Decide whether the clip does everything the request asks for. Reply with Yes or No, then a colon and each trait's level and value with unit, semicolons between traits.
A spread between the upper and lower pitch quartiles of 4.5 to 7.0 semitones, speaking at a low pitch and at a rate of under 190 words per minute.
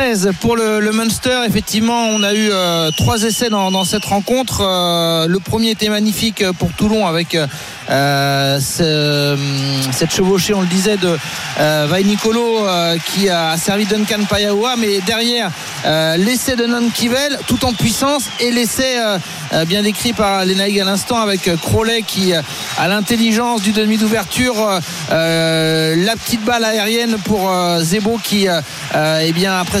No: average, 4.9 semitones; high, 200 Hz; average, 160 wpm